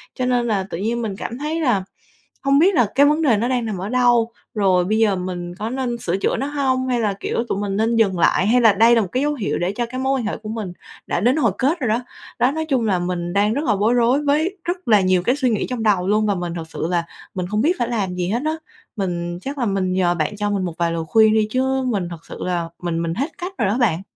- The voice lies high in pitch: Yes, high, 220 Hz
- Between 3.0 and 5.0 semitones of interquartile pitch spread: No, wide, 5.4 semitones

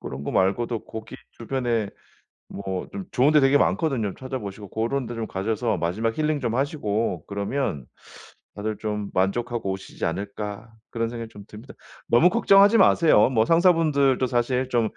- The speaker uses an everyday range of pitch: Yes, average, 4.6 semitones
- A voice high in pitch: No, low, 115 Hz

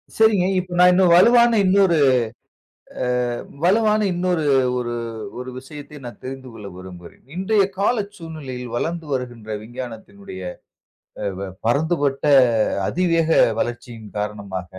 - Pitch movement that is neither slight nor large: No, wide, 7.4 semitones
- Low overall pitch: No, medium, 145 Hz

